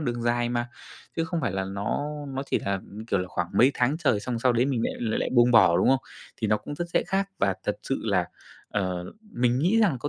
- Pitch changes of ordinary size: Yes, average, 4.9 semitones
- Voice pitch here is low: Yes, low, 120 Hz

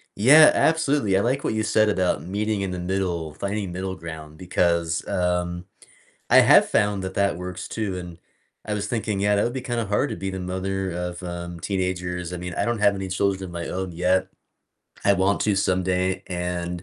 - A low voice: Yes, very low, 95 Hz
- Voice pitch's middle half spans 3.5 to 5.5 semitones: No, narrow, 2.4 semitones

